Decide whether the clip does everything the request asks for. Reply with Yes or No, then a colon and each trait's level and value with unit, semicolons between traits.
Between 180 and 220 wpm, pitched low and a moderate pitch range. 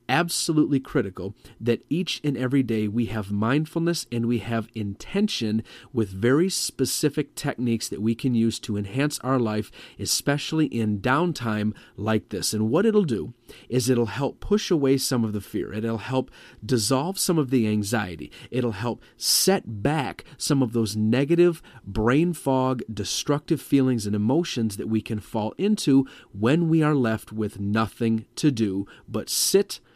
No: average, 160 wpm; low, 120 Hz; average, 5.0 semitones